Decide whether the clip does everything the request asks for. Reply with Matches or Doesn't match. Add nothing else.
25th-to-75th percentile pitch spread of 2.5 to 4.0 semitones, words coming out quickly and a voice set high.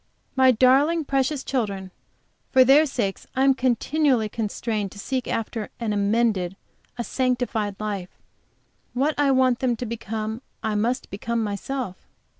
Doesn't match